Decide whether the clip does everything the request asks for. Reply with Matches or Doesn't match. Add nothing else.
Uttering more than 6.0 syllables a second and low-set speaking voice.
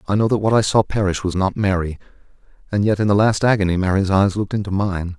Matches